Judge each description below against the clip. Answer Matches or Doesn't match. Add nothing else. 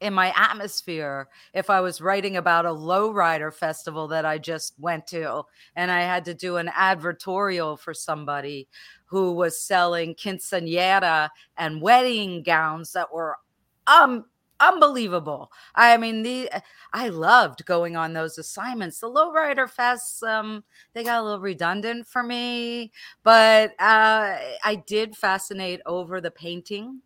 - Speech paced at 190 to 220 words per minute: Doesn't match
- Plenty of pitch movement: Doesn't match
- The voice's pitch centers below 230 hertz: Matches